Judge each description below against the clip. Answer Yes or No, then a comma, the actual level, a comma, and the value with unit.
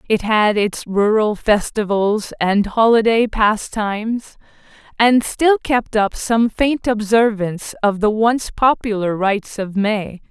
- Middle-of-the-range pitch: No, high, 215 Hz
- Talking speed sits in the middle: No, slow, 130 wpm